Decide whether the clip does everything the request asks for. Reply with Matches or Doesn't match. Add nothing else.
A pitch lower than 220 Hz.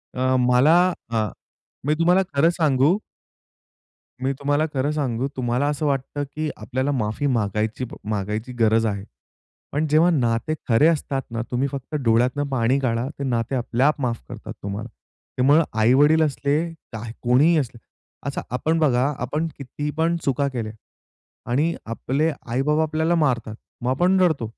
Matches